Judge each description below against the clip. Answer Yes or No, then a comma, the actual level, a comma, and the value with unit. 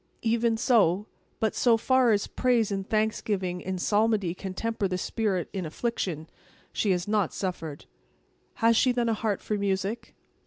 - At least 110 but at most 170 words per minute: Yes, average, 160 wpm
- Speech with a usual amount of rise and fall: Yes, average, 3.4 semitones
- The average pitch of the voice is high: Yes, high, 210 Hz